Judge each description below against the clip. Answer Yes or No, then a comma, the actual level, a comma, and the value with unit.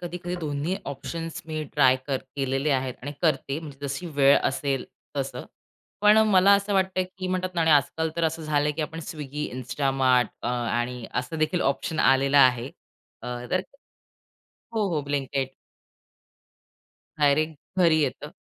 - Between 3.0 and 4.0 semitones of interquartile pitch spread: Yes, average, 3.5 semitones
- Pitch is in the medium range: Yes, medium, 145 Hz